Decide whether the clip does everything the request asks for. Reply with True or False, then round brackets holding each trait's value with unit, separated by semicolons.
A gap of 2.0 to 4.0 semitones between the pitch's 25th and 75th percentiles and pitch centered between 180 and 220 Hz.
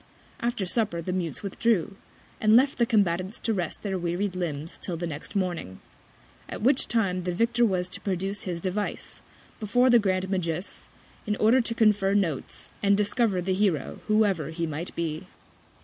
True (3.5 semitones; 190 Hz)